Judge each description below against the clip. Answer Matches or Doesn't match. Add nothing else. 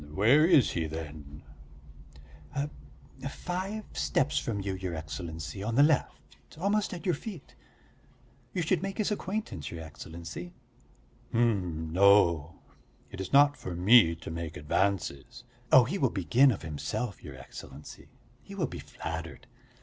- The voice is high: Doesn't match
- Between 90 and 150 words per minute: Matches